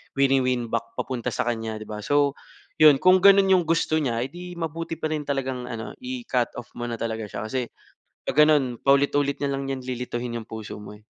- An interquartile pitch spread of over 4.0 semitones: Yes, average, 4.7 semitones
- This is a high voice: No, low, 135 Hz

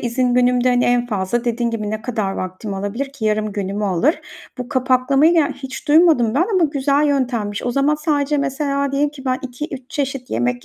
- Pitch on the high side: Yes, very high, 255 Hz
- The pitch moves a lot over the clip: No, average, 4.3 semitones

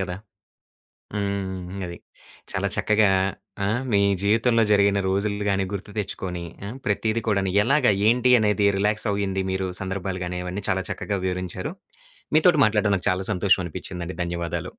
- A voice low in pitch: Yes, low, 100 Hz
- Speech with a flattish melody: Yes, narrow, 2.2 semitones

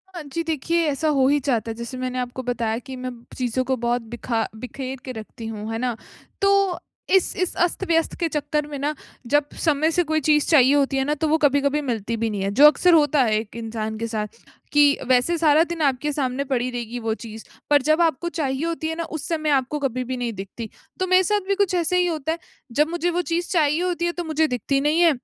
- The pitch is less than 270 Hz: No, very high, 285 Hz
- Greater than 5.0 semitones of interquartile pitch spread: No, average, 4.7 semitones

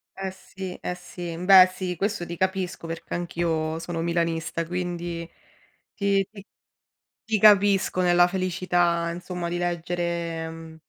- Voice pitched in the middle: Yes, medium, 175 Hz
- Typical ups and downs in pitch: No, narrow, 1.7 semitones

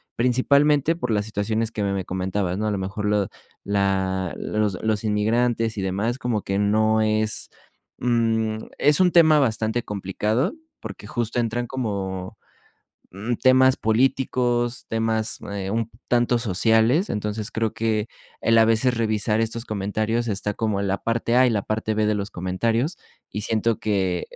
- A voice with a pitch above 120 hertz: No, low, 110 Hz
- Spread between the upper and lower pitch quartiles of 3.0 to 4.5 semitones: No, narrow, 2.6 semitones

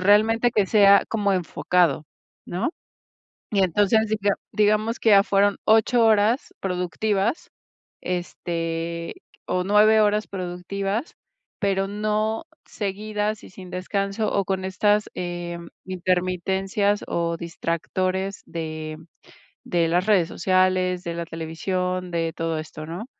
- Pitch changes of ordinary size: Yes, average, 3.0 semitones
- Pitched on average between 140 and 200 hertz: Yes, high, 190 Hz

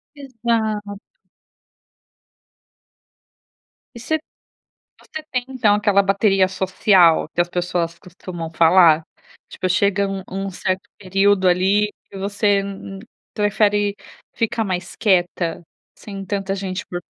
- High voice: Yes, high, 195 Hz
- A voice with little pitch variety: Yes, narrow, 2.1 semitones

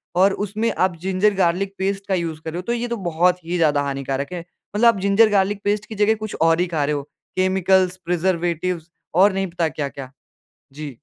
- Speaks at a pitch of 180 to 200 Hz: Yes, medium, 185 Hz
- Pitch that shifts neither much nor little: Yes, average, 3.3 semitones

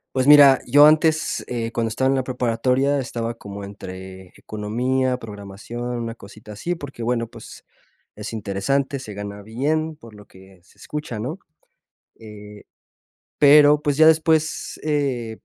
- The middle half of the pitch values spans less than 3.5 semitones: No, average, 5.2 semitones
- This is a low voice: Yes, low, 120 Hz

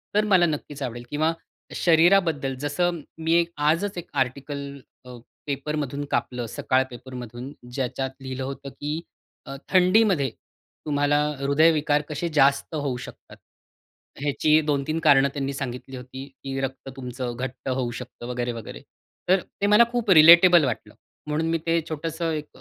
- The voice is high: No, medium, 145 Hz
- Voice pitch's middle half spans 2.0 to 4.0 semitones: Yes, average, 3.6 semitones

